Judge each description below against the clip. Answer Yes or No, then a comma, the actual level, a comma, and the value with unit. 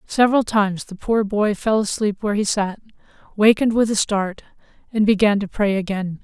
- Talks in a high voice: Yes, high, 205 Hz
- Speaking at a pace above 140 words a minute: Yes, average, 185 wpm